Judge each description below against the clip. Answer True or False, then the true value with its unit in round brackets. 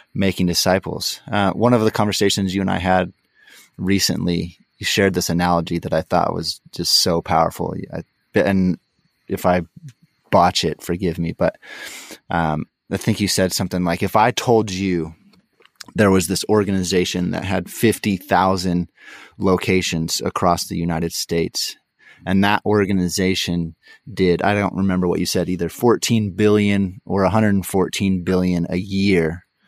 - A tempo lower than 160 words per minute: True (150 wpm)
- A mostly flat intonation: True (2.3 semitones)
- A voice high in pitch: False (95 Hz)